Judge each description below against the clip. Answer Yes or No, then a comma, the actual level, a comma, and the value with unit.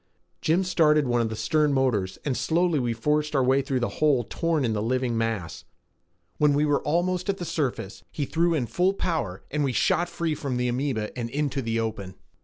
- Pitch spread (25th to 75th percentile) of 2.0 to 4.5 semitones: No, average, 5.0 semitones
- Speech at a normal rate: No, fast, 210 wpm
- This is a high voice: No, medium, 140 Hz